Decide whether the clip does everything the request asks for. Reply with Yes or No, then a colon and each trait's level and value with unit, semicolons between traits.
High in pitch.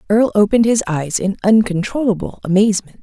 Yes: high, 205 Hz